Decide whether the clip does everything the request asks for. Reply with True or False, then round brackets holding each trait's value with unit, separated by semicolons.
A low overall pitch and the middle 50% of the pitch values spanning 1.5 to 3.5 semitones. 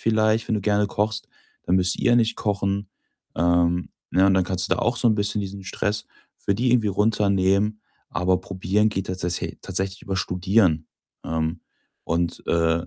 True (100 Hz; 2.7 semitones)